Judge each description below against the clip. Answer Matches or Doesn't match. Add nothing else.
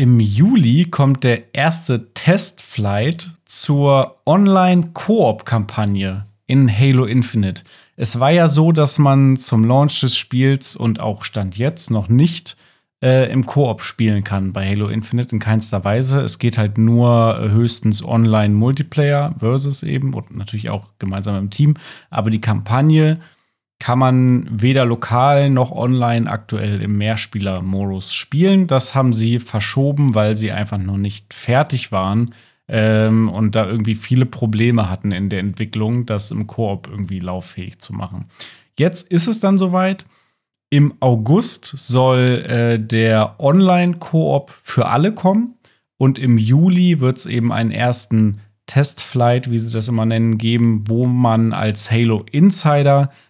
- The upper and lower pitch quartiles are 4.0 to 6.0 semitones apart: Matches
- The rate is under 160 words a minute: Matches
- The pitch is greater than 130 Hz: Doesn't match